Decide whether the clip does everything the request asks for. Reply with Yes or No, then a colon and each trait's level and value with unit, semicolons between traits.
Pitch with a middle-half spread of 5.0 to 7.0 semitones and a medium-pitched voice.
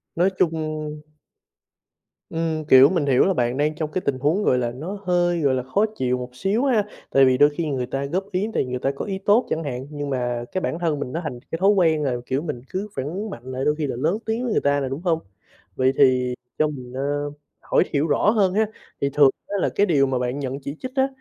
Yes: wide, 5.4 semitones; medium, 150 Hz